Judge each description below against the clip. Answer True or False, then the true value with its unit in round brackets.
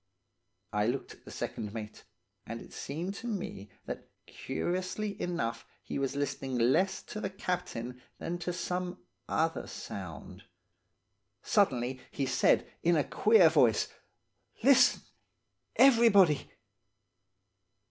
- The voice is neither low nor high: True (170 Hz)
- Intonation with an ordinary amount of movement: False (7.3 semitones)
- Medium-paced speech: False (115 wpm)